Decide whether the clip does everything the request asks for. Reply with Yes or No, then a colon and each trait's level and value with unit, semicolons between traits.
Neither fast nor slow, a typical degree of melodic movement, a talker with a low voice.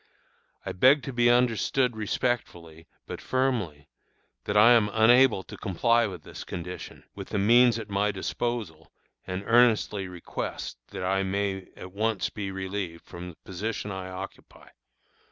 Yes: average, 150 wpm; average, 4.3 semitones; low, 100 Hz